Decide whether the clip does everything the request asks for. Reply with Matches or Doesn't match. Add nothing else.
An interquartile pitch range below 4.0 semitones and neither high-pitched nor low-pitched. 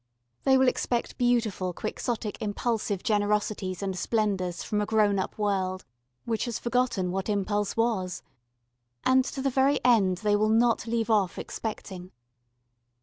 Doesn't match